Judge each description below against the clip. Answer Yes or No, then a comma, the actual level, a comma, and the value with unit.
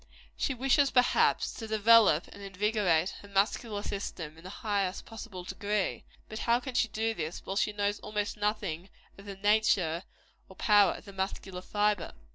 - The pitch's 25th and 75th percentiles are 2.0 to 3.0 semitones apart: Yes, narrow, 2.4 semitones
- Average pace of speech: Yes, average, 170 wpm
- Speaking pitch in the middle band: No, high, 205 Hz